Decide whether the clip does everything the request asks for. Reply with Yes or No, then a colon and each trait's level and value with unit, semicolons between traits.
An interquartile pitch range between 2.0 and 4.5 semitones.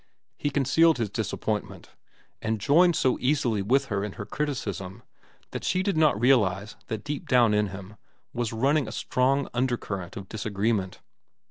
No: average, 5.3 semitones